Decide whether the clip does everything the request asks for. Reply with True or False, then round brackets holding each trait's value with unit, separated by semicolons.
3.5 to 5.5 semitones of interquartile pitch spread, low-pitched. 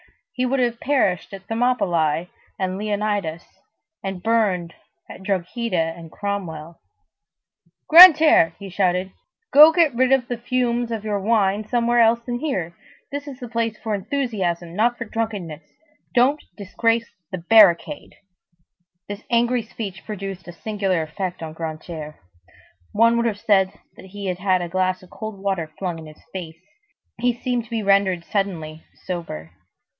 False (4.7 semitones; 200 Hz)